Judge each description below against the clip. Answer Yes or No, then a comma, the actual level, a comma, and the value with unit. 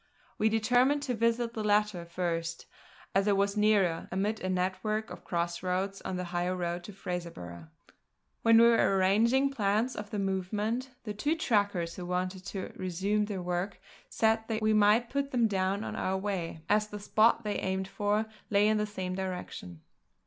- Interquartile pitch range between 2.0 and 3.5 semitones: Yes, average, 3.0 semitones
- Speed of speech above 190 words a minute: No, average, 180 wpm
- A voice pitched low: No, high, 200 Hz